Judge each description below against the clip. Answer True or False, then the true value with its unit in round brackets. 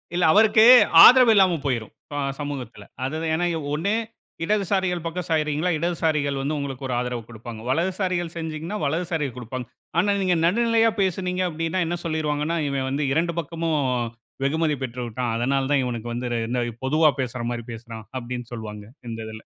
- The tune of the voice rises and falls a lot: True (5.7 semitones)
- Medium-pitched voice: True (150 Hz)